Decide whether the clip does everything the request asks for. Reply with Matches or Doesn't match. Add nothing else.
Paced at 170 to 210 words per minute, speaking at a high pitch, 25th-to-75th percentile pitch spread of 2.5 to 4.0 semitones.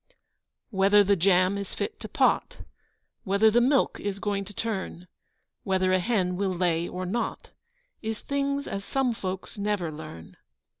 Doesn't match